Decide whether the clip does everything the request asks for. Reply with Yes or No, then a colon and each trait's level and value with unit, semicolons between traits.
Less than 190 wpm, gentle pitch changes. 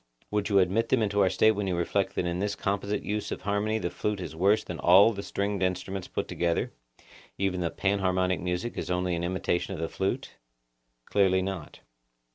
No: average, 200 wpm; narrow, 2.2 semitones